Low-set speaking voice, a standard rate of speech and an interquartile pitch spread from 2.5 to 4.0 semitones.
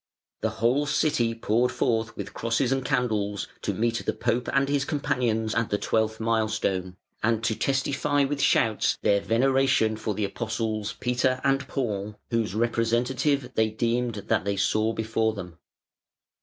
Yes: low, 115 Hz; average, 155 wpm; average, 2.8 semitones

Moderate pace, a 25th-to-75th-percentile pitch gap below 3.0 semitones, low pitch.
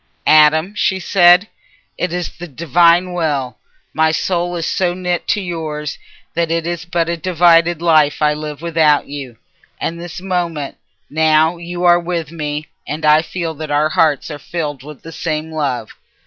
No: average, 170 wpm; narrow, 2.4 semitones; medium, 165 Hz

